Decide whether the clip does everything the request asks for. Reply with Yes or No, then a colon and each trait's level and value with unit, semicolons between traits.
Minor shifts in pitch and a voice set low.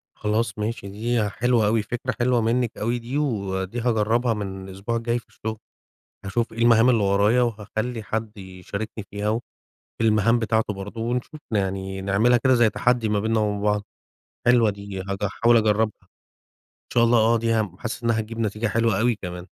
Yes: narrow, 2.3 semitones; low, 110 Hz